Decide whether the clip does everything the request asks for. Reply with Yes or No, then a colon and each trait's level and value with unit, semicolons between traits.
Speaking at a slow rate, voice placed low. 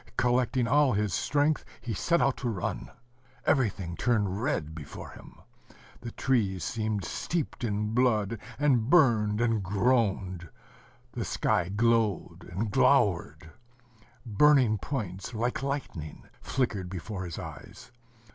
Yes: slow, 120 wpm; low, 110 Hz